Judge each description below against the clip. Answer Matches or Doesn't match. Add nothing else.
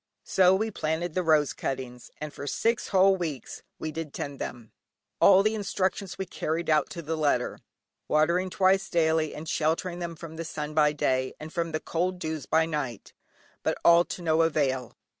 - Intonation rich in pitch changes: Doesn't match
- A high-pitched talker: Doesn't match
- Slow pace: Doesn't match